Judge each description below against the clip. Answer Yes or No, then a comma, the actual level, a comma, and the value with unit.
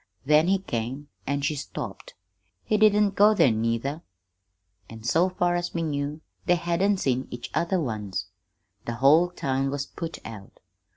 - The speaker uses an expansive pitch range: Yes, wide, 6.3 semitones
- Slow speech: No, average, 160 wpm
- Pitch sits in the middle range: Yes, medium, 145 Hz